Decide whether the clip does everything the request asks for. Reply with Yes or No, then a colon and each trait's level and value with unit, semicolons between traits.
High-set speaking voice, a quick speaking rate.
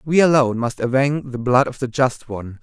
No: low, 130 Hz; fast, 230 wpm